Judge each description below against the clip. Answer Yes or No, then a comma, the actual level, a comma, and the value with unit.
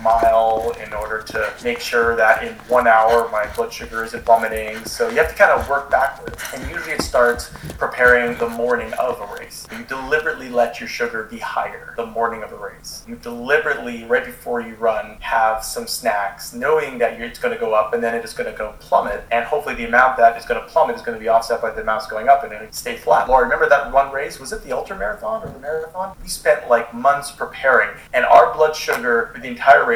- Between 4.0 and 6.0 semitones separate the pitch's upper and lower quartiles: No, average, 3.5 semitones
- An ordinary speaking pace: No, fast, 235 wpm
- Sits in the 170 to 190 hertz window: No, low, 120 Hz